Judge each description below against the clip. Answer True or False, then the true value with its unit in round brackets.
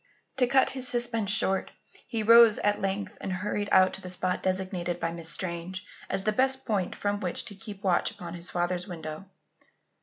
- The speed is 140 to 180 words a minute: False (190 wpm)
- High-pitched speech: True (195 Hz)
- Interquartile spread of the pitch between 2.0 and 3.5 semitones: True (3.1 semitones)